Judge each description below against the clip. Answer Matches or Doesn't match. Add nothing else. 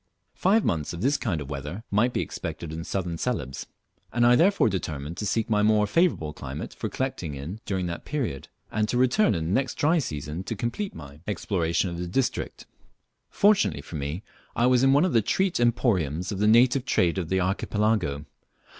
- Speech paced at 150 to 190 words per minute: Doesn't match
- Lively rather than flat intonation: Matches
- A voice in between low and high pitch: Doesn't match